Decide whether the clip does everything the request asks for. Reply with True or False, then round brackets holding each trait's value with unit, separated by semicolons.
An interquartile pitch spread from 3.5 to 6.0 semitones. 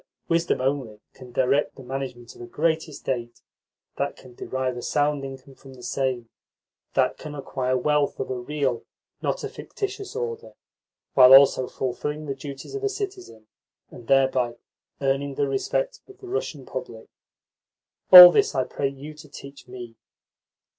False (3.0 semitones)